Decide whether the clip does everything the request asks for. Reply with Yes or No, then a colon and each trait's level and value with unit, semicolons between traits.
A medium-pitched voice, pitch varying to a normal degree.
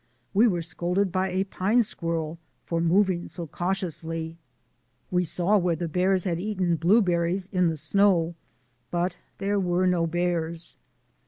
No: medium, 175 Hz; narrow, 2.2 semitones